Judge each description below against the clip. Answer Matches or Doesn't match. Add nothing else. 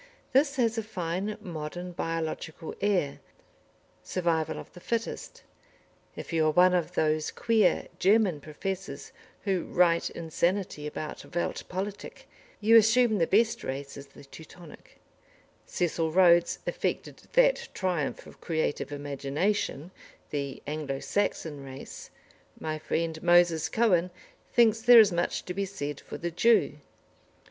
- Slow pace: Matches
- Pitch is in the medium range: Matches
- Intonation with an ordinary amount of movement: Matches